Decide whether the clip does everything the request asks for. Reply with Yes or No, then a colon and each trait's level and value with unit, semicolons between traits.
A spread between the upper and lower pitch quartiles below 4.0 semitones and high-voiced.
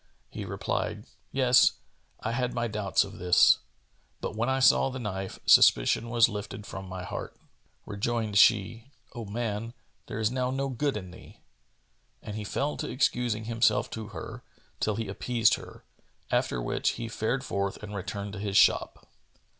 No: average, 3.0 semitones; low, 110 Hz